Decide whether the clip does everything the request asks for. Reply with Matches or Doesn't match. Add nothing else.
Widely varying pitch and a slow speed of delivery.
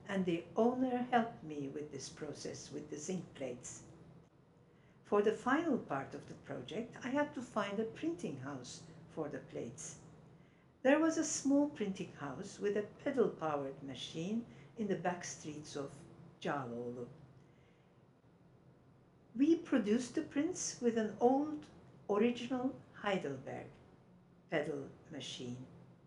Matches